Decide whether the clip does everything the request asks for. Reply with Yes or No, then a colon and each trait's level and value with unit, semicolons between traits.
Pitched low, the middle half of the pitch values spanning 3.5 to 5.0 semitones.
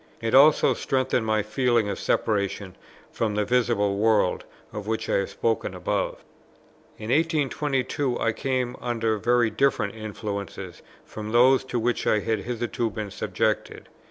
No: low, 115 Hz; average, 2.9 semitones